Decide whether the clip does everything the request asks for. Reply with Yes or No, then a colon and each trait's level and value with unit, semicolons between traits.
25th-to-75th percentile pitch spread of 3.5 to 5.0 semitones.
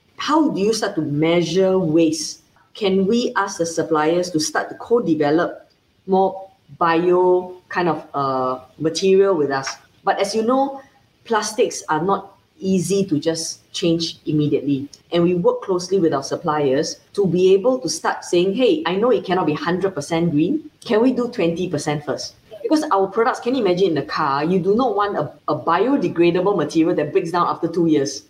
Yes: average, 3.9 semitones